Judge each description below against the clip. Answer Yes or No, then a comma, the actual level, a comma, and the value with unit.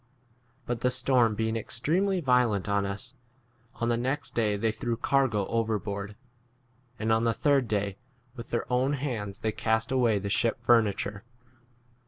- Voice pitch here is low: Yes, low, 115 Hz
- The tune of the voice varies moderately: Yes, average, 3.2 semitones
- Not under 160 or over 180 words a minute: Yes, average, 170 wpm